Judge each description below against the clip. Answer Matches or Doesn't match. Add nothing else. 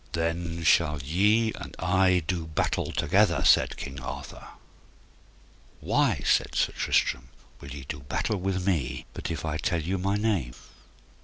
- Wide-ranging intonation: Doesn't match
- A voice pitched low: Matches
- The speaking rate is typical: Matches